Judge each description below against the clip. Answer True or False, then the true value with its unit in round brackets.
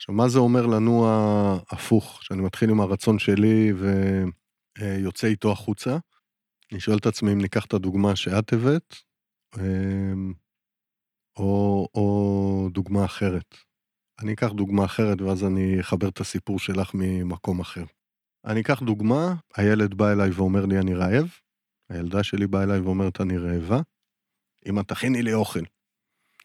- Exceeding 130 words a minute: True (140 wpm)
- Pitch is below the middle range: True (100 Hz)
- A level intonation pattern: True (2.3 semitones)